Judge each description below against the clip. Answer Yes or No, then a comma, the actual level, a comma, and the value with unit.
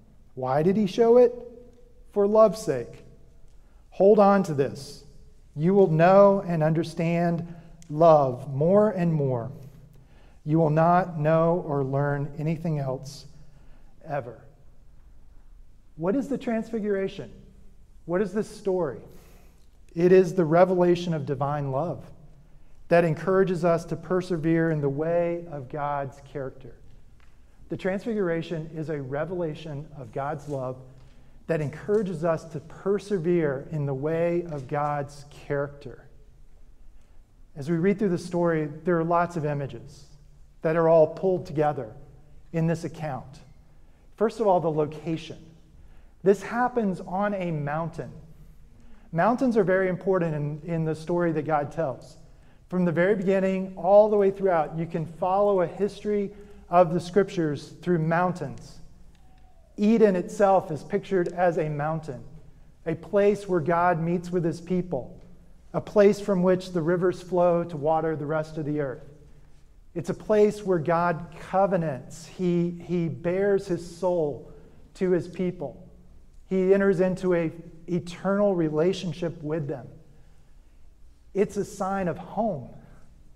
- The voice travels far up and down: No, average, 3.9 semitones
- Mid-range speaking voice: Yes, medium, 165 Hz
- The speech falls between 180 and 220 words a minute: No, slow, 135 wpm